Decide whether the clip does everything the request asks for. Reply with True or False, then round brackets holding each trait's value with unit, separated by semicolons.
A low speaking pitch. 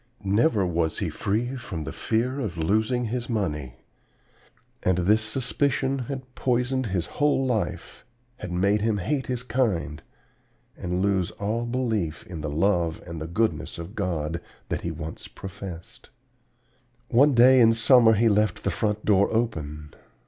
True (105 Hz)